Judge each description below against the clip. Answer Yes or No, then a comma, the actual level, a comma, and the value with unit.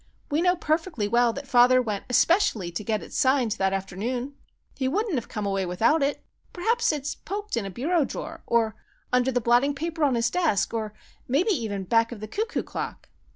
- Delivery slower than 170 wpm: No, average, 200 wpm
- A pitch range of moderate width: No, wide, 6.2 semitones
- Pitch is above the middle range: Yes, very high, 250 Hz